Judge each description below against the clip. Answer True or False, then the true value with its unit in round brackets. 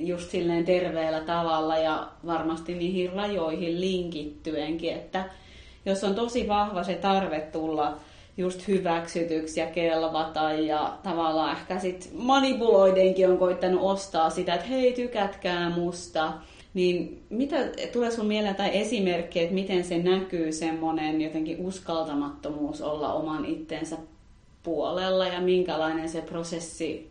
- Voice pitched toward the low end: False (175 Hz)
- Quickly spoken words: False (125 wpm)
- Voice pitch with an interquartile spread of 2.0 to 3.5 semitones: True (2.8 semitones)